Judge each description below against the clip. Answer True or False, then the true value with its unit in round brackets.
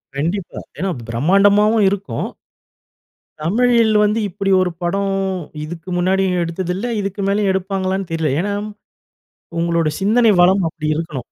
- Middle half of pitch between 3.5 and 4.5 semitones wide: False (3.1 semitones)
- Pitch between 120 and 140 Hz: False (190 Hz)